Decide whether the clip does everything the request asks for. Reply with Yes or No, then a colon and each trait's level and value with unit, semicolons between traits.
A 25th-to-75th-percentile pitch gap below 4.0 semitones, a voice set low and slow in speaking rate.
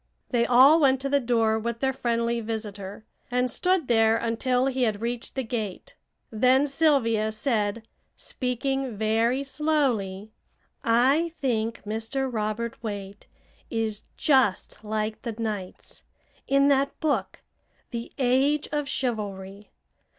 No: average, 3.6 semitones; high, 235 Hz; slow, 125 wpm